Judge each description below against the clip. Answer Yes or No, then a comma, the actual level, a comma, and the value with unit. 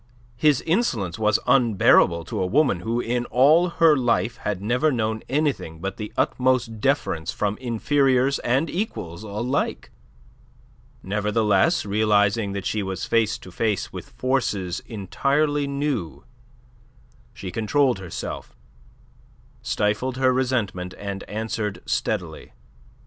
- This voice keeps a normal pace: No, slow, 120 wpm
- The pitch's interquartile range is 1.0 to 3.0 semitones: No, average, 4.8 semitones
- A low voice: Yes, low, 115 Hz